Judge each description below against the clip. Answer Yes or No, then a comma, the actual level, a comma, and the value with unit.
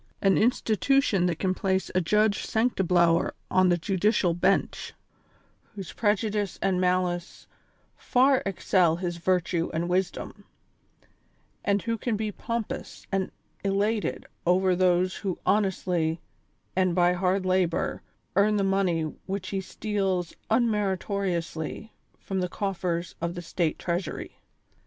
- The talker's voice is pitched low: No, high, 190 Hz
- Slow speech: Yes, slow, 125 wpm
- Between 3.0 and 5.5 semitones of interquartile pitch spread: No, narrow, 2.5 semitones